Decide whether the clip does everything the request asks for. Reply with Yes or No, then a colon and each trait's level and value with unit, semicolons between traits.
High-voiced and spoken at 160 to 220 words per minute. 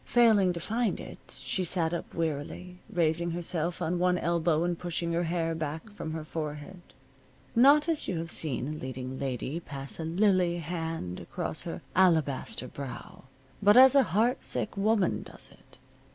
No: medium, 170 Hz; average, 165 wpm